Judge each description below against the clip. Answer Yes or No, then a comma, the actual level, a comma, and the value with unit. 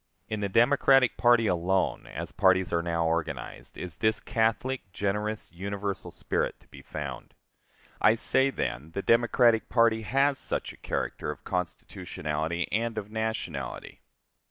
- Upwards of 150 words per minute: No, average, 140 wpm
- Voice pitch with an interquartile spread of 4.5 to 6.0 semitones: Yes, average, 5.1 semitones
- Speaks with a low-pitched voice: Yes, low, 105 Hz